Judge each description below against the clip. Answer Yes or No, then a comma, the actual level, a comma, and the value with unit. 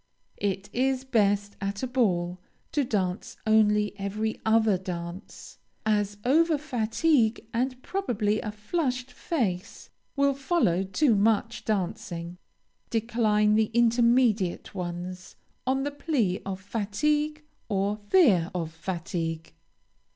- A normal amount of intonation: Yes, average, 4.7 semitones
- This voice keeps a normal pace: No, slow, 115 wpm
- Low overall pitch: No, high, 215 Hz